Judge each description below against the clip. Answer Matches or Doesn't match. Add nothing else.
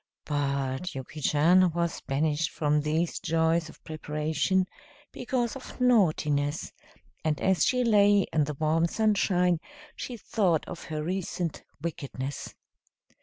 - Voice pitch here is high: Doesn't match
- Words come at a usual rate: Doesn't match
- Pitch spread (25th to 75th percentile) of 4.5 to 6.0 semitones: Doesn't match